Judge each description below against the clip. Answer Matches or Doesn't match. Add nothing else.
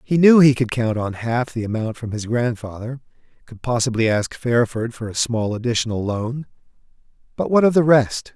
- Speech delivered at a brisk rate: Doesn't match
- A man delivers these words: Matches